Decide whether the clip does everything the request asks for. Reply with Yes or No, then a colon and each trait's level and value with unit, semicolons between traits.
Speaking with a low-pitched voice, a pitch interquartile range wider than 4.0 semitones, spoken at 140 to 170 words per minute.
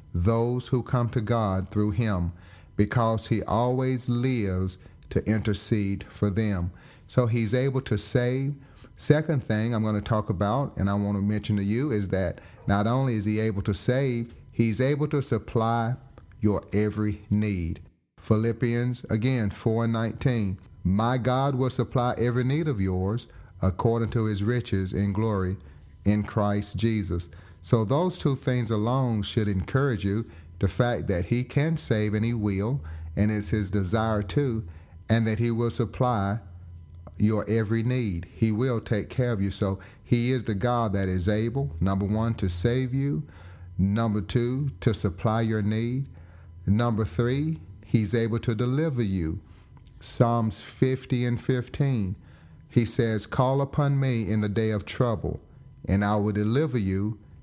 No: low, 110 Hz; average, 3.6 semitones; average, 160 wpm